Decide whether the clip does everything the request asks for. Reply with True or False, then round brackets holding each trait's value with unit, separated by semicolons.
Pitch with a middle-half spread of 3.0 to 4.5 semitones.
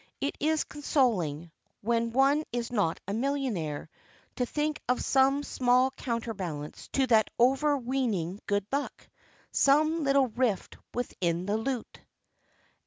False (5.2 semitones)